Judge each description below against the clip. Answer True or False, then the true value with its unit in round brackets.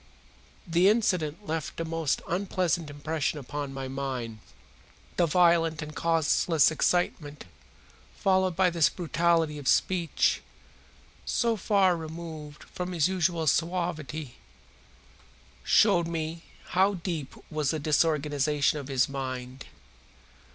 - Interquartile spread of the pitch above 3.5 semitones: False (3.1 semitones)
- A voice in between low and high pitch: True (160 Hz)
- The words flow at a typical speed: False (110 wpm)